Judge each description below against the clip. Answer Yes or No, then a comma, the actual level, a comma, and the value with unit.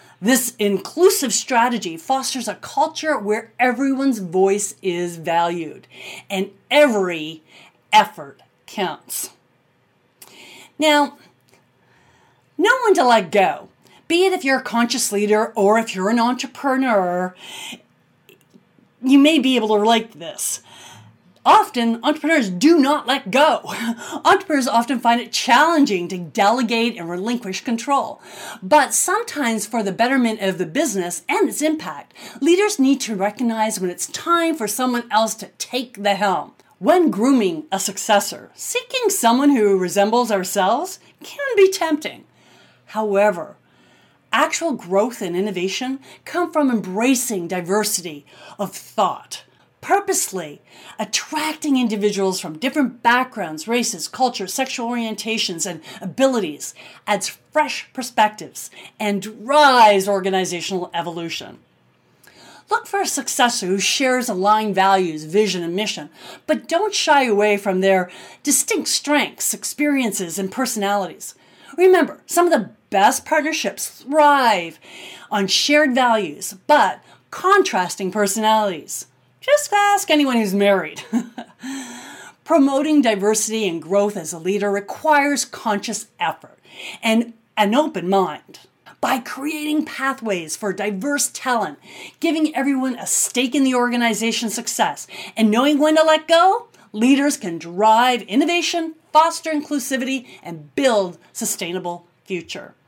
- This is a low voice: No, high, 235 Hz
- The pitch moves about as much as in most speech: No, wide, 6.4 semitones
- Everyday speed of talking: No, slow, 120 wpm